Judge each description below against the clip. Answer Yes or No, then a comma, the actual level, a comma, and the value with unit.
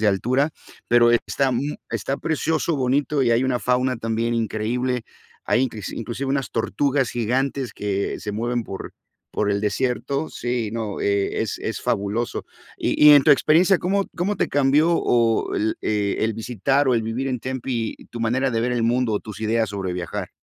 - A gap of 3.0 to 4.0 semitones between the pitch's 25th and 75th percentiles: Yes, average, 3.4 semitones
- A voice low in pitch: Yes, low, 120 Hz